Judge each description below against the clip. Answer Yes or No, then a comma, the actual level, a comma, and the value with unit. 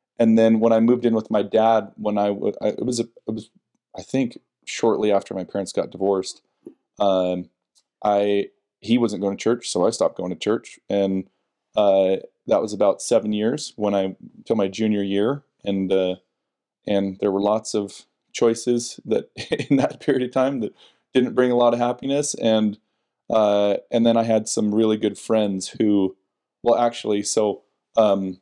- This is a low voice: Yes, low, 105 Hz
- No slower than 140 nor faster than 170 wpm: No, average, 180 wpm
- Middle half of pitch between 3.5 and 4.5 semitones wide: No, average, 2.9 semitones